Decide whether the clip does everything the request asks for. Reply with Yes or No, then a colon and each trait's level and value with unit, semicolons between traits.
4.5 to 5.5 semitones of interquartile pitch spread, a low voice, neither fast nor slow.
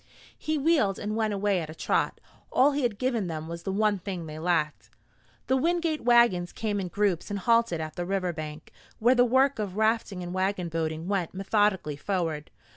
No: average, 5.2 semitones; high, 195 Hz; average, 195 wpm